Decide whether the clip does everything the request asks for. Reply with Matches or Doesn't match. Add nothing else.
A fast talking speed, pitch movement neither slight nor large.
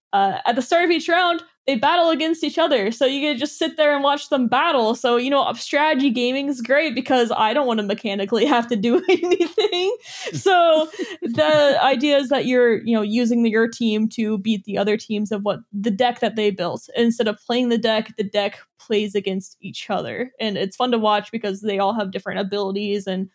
Doesn't match